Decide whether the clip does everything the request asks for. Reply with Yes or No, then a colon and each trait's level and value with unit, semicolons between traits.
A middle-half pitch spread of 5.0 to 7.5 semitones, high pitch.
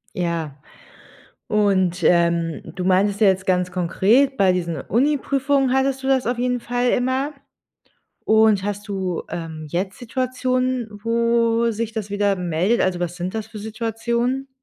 Yes: average, 5.3 semitones; high, 215 Hz